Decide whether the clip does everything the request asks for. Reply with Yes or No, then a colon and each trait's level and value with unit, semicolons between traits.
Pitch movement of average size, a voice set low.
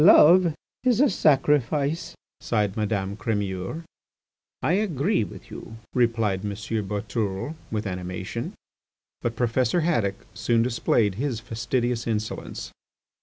No: wide, 5.8 semitones; low, 115 Hz